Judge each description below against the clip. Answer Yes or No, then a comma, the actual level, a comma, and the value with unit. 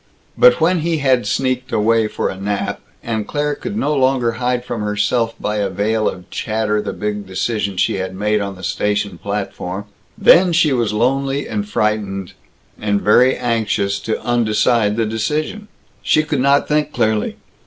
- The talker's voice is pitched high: No, low, 110 Hz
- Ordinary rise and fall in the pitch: Yes, average, 4.4 semitones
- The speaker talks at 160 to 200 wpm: Yes, average, 170 wpm